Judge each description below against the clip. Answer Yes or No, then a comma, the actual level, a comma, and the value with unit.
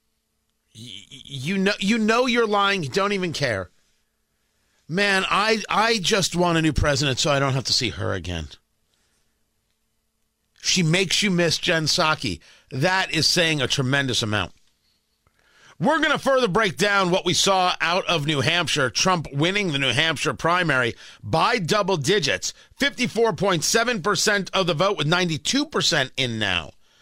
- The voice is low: No, medium, 175 Hz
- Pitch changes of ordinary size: No, wide, 6.3 semitones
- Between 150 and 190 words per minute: Yes, average, 160 wpm